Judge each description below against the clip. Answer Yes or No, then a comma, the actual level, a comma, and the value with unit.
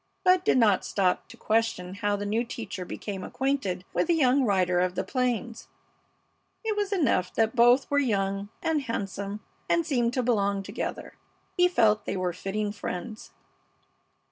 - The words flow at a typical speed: Yes, average, 165 wpm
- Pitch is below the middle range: No, high, 220 Hz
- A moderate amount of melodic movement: Yes, average, 4.7 semitones